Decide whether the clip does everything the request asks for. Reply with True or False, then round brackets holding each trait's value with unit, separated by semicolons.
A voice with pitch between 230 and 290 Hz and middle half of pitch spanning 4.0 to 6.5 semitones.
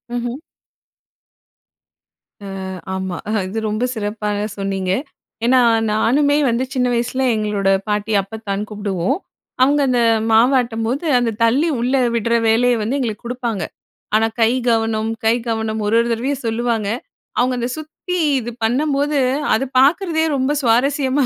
False (235 Hz; 3.2 semitones)